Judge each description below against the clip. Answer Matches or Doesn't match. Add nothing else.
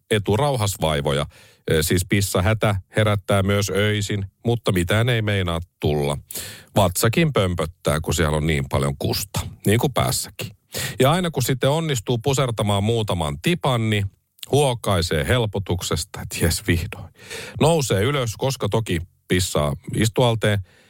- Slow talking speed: Doesn't match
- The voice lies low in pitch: Matches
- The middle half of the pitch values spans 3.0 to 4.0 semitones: Doesn't match